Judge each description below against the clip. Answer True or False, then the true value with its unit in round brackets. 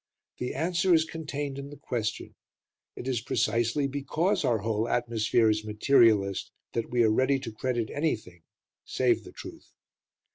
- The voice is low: True (120 Hz)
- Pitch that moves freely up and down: False (4.4 semitones)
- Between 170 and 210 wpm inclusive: False (150 wpm)